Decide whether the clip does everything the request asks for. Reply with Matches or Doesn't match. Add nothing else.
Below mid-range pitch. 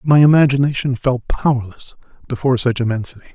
Matches